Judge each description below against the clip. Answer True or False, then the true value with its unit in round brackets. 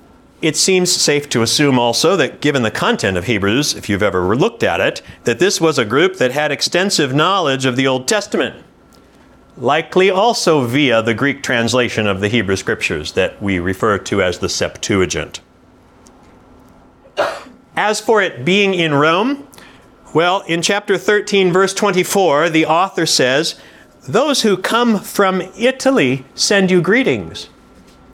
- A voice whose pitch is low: False (160 Hz)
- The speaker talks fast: False (150 wpm)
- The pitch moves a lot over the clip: True (7.5 semitones)